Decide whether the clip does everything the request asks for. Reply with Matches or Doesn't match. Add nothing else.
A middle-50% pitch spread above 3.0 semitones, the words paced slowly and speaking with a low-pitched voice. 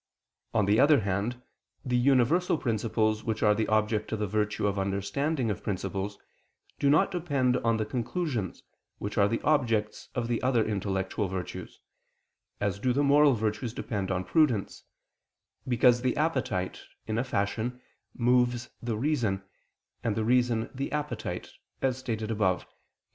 Doesn't match